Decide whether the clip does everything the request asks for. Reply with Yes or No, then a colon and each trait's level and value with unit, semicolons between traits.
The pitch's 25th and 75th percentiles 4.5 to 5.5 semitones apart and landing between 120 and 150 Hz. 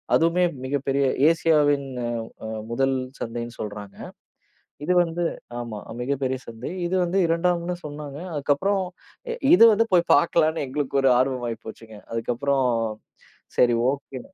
Yes: average, 5.2 semitones; medium, 140 Hz